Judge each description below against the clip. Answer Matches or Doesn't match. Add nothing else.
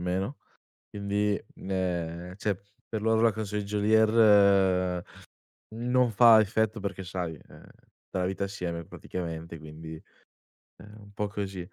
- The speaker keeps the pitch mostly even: Doesn't match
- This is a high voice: Doesn't match